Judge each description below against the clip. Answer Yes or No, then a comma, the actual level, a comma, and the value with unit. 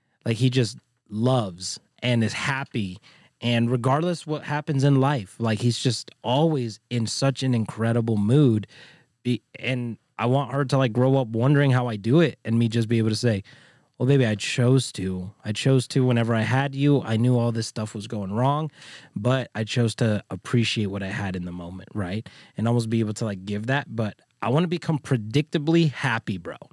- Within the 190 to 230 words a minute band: Yes, average, 200 wpm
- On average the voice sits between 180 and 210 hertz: No, low, 120 Hz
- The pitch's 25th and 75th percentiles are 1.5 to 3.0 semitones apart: No, average, 3.7 semitones